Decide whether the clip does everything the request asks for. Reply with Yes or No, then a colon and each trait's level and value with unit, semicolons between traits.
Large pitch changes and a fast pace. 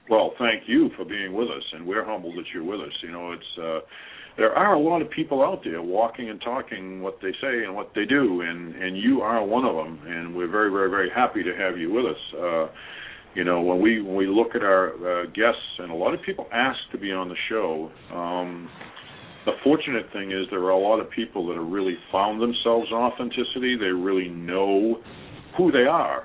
No: average, 4.7 semitones; fast, 230 wpm